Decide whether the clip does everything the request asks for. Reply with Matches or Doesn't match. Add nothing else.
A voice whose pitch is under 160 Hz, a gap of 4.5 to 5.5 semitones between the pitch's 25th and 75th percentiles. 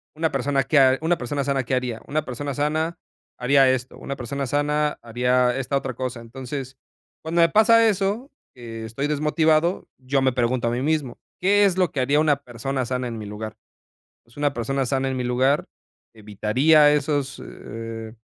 Doesn't match